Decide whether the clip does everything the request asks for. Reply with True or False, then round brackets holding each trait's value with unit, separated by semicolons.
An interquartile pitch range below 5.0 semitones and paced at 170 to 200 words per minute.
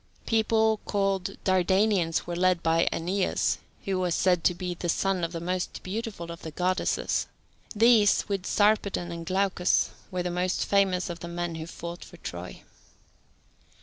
False (2.5 semitones; 160 wpm)